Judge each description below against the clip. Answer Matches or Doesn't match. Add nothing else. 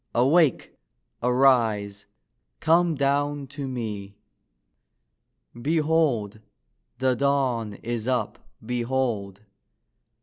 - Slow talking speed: Matches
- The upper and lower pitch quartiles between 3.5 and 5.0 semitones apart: Matches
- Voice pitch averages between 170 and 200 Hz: Doesn't match